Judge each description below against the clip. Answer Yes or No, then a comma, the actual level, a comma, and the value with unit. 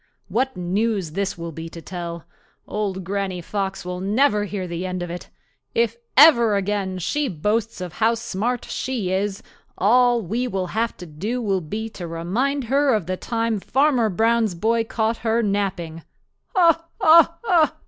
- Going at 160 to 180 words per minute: Yes, average, 165 wpm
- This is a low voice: No, high, 205 Hz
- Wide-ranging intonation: No, average, 4.3 semitones